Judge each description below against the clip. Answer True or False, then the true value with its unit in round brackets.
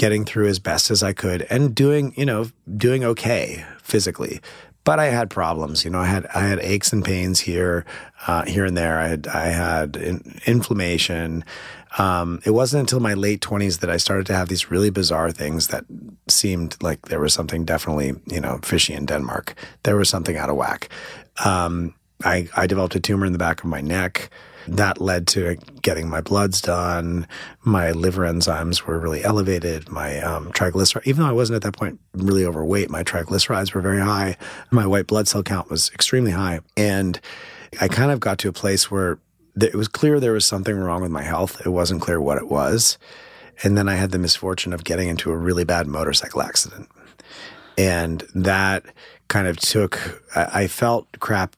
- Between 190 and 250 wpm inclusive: True (195 wpm)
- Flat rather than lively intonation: False (3.3 semitones)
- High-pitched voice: False (95 Hz)